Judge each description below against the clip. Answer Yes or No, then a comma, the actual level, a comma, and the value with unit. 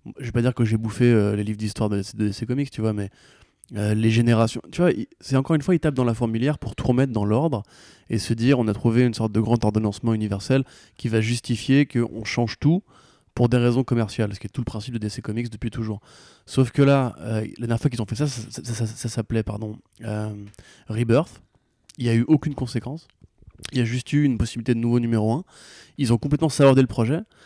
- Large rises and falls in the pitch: No, average, 3.0 semitones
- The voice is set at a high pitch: No, low, 120 Hz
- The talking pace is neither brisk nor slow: No, fast, 250 wpm